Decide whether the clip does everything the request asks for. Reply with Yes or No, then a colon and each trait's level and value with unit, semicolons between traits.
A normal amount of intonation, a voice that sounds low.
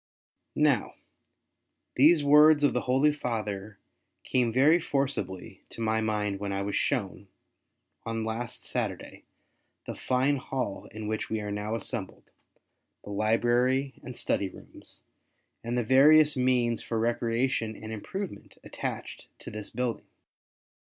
Yes: average, 3.7 semitones; low, 120 Hz